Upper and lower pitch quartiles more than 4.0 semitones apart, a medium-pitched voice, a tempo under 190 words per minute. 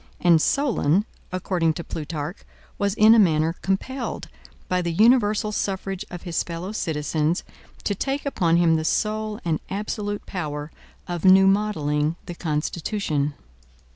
Yes: average, 4.5 semitones; medium, 180 Hz; average, 140 wpm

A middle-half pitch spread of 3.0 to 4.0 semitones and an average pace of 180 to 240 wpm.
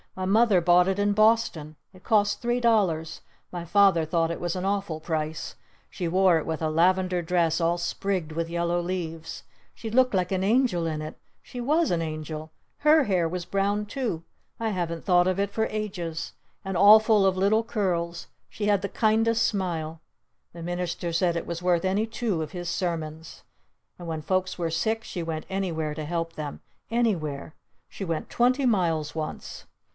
Yes: average, 3.7 semitones; average, 185 wpm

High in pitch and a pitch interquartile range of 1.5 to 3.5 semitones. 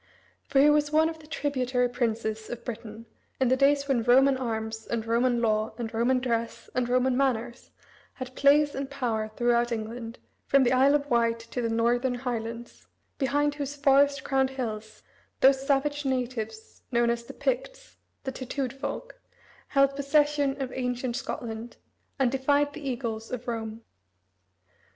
Yes: very high, 255 Hz; average, 3.0 semitones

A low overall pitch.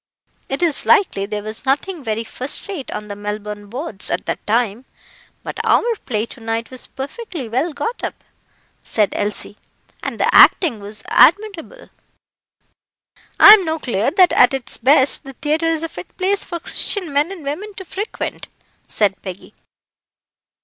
No: very high, 270 Hz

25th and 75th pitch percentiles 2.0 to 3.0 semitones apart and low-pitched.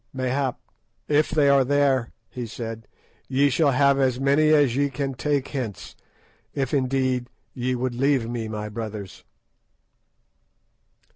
Yes: narrow, 2.6 semitones; low, 130 Hz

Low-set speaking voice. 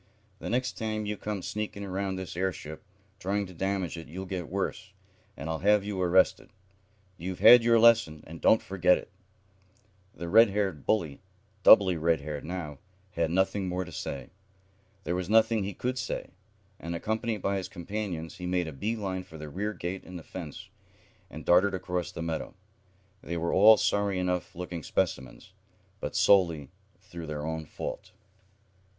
Yes: very low, 95 Hz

